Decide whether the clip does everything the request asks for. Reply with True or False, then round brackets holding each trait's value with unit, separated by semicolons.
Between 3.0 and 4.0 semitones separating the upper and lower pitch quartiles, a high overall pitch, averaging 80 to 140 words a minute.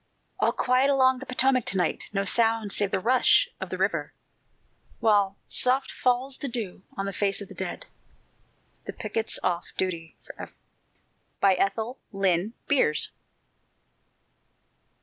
False (4.6 semitones; 220 Hz; 135 wpm)